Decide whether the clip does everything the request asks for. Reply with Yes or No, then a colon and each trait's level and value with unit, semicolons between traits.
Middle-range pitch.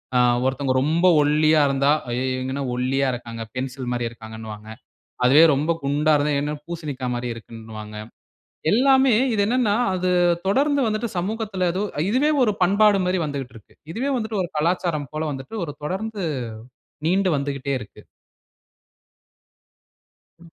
Yes: medium, 150 Hz